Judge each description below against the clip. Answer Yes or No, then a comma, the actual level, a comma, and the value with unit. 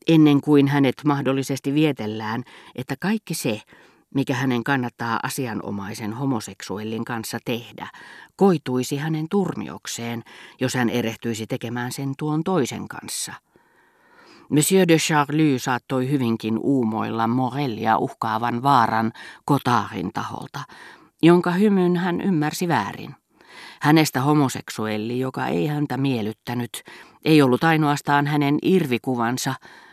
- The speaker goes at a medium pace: Yes, average, 105 wpm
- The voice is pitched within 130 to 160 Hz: Yes, low, 135 Hz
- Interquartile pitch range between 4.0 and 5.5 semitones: Yes, average, 4.5 semitones